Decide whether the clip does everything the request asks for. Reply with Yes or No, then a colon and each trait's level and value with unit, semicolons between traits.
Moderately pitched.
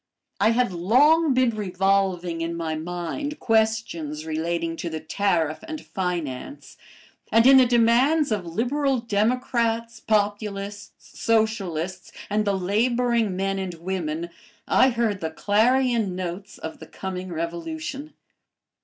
No: high, 205 Hz